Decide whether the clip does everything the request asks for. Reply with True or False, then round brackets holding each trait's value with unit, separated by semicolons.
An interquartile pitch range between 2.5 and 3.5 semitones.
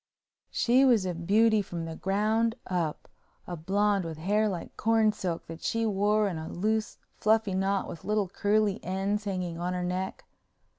True (3.1 semitones)